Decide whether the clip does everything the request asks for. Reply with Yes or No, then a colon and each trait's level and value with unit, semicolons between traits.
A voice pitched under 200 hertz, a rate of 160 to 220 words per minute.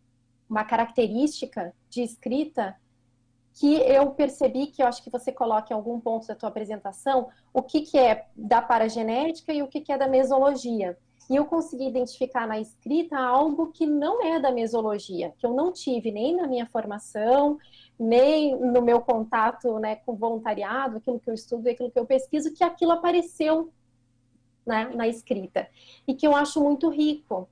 No: high, 245 Hz; average, 175 wpm